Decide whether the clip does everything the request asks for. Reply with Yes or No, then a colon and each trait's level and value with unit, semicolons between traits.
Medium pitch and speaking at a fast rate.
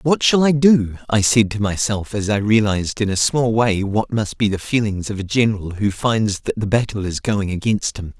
No: low, 105 Hz; fast, 235 wpm